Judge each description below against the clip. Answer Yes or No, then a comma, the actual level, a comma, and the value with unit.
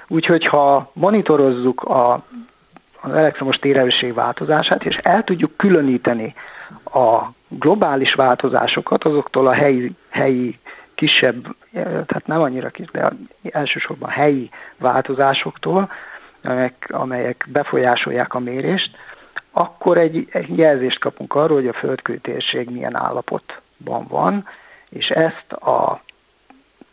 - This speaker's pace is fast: No, average, 110 wpm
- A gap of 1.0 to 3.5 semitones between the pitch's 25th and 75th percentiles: No, average, 4.0 semitones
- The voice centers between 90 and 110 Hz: No, medium, 140 Hz